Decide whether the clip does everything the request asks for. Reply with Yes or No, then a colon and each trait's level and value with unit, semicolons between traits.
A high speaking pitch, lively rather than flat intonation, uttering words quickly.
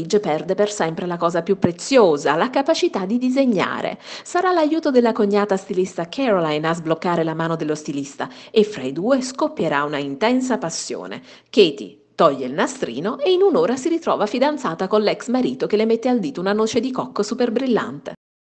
Yes: high, 210 Hz; wide, 7.3 semitones; fast, 180 wpm